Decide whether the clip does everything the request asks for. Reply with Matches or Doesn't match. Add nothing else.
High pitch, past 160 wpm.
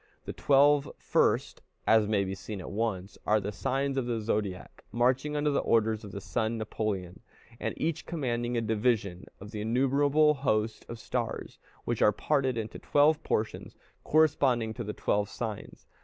Doesn't match